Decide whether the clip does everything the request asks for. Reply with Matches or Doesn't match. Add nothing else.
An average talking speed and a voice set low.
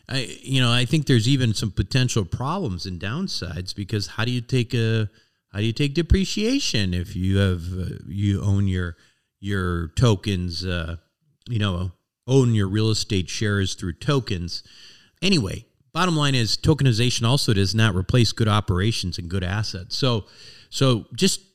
Matches